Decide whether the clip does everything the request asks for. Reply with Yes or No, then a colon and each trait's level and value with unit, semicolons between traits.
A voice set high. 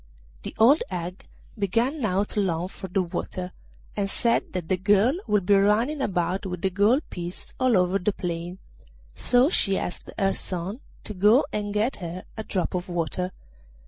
Yes: high, 195 Hz